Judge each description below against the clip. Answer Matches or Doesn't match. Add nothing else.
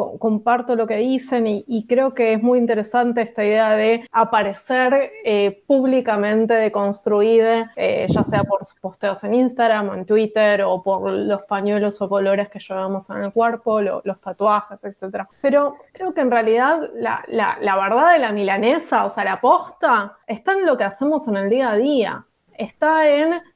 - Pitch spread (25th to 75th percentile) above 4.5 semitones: Doesn't match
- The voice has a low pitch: Doesn't match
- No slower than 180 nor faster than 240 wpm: Matches